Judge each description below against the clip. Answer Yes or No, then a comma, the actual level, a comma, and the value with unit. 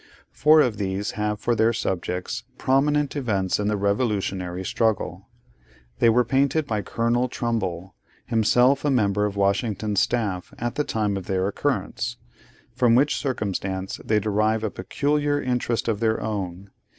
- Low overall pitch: Yes, low, 110 Hz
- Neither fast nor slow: Yes, average, 150 wpm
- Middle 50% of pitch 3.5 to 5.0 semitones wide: Yes, average, 3.8 semitones